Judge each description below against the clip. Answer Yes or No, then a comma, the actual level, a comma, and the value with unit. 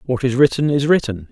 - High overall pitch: No, low, 130 Hz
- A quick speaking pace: Yes, fast, 225 wpm